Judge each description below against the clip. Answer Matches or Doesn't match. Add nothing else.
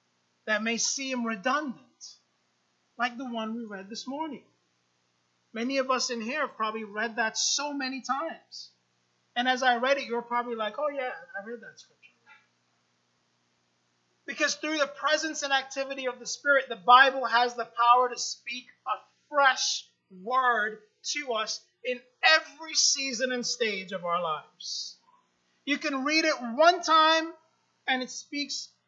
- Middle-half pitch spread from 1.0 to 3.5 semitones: Doesn't match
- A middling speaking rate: Matches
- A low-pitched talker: Doesn't match